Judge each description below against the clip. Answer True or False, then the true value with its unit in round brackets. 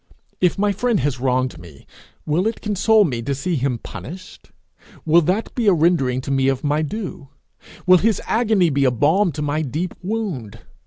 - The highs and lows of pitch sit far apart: True (6.6 semitones)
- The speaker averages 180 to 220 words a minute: True (190 wpm)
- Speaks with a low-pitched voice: False (155 Hz)